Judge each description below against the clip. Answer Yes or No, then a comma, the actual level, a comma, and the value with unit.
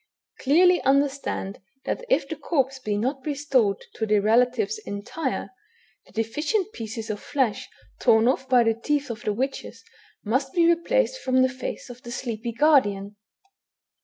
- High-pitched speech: Yes, very high, 260 Hz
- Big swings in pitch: No, average, 4.6 semitones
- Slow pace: No, average, 155 wpm